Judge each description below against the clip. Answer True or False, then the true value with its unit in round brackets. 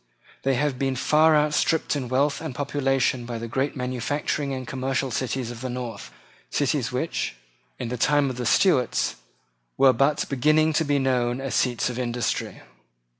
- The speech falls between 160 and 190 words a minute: True (170 wpm)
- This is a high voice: False (130 Hz)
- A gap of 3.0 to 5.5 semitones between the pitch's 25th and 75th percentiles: False (2.6 semitones)